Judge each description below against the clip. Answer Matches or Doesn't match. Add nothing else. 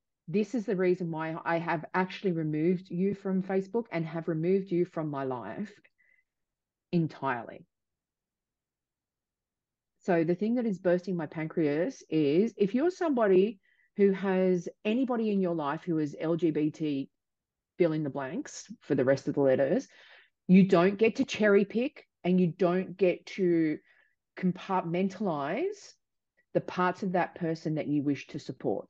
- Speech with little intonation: Doesn't match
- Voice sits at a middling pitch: Matches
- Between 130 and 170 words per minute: Matches